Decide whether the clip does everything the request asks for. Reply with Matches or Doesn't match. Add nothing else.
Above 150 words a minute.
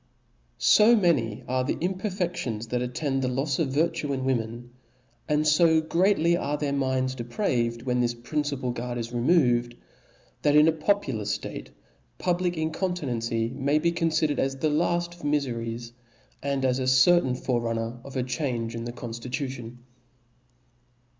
Matches